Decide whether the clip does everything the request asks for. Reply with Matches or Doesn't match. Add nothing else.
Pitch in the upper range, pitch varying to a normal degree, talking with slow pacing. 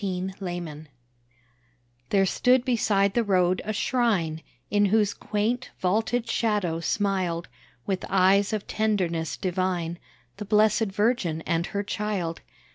Matches